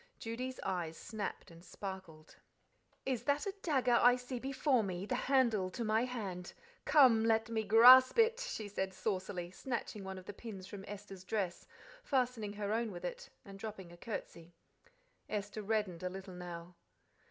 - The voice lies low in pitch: No, high, 210 Hz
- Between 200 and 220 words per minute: No, average, 170 wpm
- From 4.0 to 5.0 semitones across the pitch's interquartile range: Yes, average, 4.6 semitones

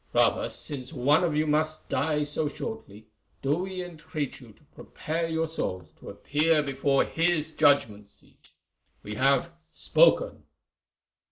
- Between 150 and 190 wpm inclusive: No, average, 140 wpm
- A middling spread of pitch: Yes, average, 3.1 semitones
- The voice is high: No, medium, 150 Hz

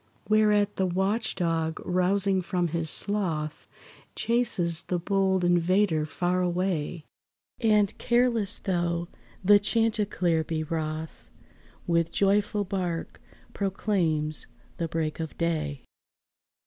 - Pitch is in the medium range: Yes, medium, 180 Hz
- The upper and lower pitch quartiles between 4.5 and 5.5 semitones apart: No, average, 3.6 semitones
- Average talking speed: No, slow, 105 wpm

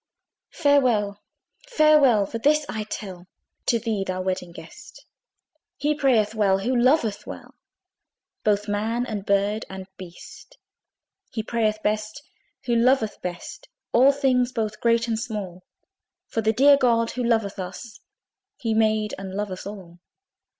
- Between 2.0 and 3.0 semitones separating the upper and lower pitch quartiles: No, average, 3.5 semitones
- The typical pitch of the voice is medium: No, high, 220 Hz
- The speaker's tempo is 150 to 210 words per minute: No, slow, 135 wpm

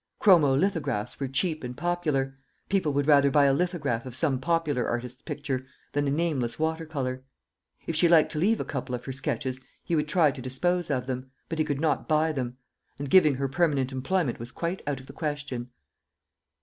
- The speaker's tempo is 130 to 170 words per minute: No, average, 200 wpm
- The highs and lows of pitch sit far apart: No, average, 3.8 semitones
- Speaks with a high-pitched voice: No, medium, 145 Hz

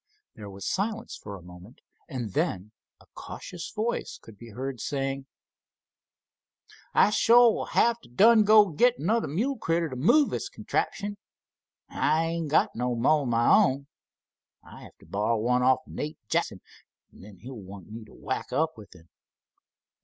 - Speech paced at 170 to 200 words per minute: Yes, average, 175 wpm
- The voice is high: No, low, 135 Hz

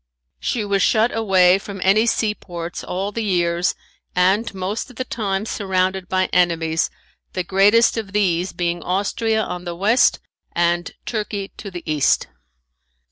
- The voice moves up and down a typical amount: Yes, average, 3.0 semitones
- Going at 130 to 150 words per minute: Yes, average, 145 wpm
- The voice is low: No, high, 190 Hz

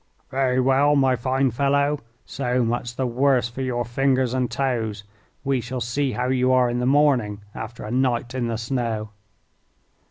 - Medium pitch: No, low, 125 Hz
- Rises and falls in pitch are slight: Yes, narrow, 2.0 semitones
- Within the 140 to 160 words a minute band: No, average, 170 wpm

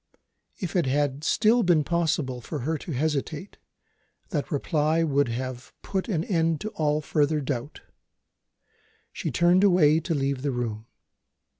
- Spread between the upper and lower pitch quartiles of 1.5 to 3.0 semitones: No, average, 3.5 semitones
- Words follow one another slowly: No, average, 145 wpm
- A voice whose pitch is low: No, medium, 150 Hz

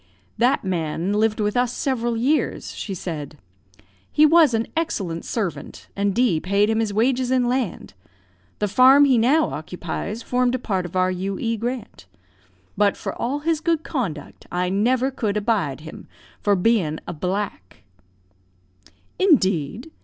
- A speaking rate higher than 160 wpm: No, average, 150 wpm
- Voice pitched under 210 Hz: No, high, 215 Hz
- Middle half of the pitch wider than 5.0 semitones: Yes, wide, 5.5 semitones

